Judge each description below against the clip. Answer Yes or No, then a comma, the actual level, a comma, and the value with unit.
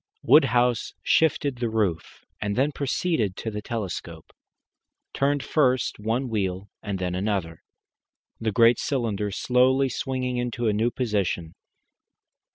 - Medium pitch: No, low, 115 Hz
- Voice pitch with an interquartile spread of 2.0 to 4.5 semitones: Yes, average, 4.0 semitones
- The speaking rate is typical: No, slow, 125 wpm